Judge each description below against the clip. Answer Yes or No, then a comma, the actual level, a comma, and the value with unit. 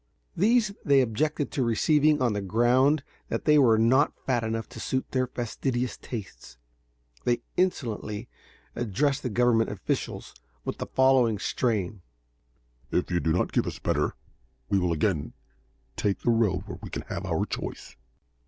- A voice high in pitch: No, low, 120 Hz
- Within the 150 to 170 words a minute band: Yes, average, 155 wpm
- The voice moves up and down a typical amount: Yes, average, 3.9 semitones